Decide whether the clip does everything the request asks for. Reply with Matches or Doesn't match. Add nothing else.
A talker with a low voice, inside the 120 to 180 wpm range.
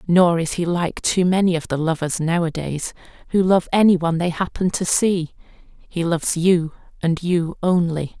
Doesn't match